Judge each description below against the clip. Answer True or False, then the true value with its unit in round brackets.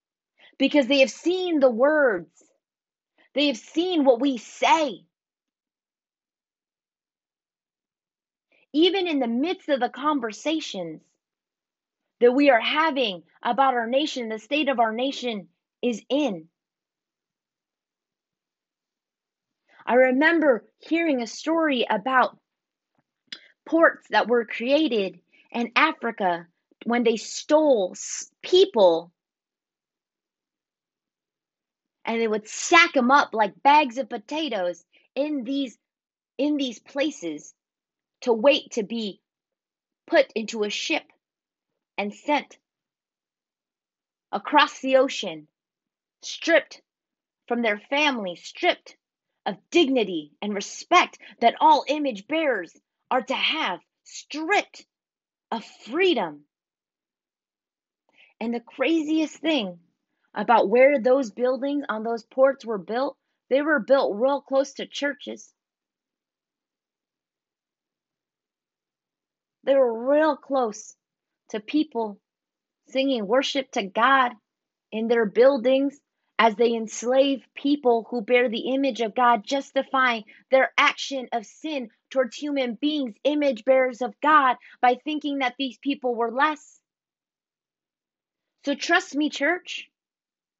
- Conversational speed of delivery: False (105 wpm)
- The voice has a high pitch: True (265 Hz)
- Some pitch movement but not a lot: True (4.0 semitones)